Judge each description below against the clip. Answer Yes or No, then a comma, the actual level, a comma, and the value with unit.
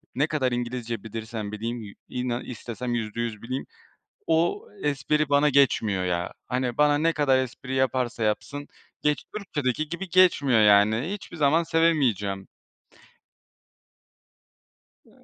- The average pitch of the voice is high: No, low, 125 Hz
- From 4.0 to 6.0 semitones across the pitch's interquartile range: Yes, average, 4.7 semitones